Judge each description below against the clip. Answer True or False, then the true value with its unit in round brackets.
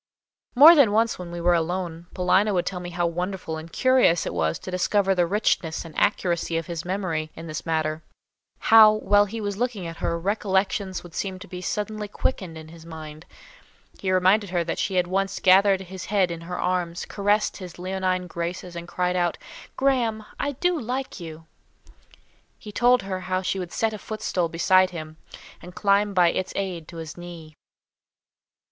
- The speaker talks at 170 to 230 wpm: True (190 wpm)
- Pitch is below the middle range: False (185 Hz)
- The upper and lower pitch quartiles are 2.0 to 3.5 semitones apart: True (3.2 semitones)